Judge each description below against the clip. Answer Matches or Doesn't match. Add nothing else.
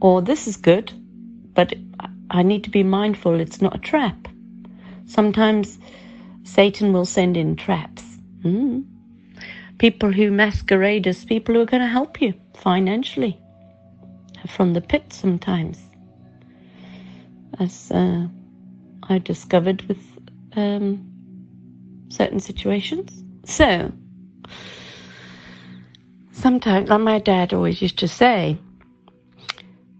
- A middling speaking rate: Doesn't match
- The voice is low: Doesn't match